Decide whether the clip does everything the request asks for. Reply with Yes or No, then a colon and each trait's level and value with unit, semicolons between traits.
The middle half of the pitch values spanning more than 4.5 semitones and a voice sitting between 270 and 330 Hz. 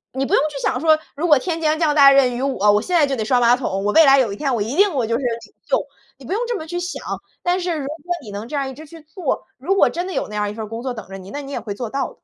Yes: wide, 5.5 semitones; very high, 275 Hz